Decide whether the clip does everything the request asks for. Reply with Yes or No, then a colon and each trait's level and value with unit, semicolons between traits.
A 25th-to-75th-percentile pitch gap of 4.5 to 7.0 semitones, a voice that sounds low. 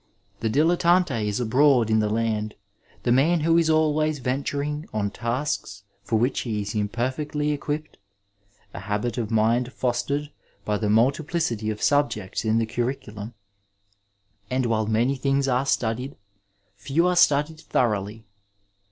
Yes: average, 5.1 semitones; low, 125 Hz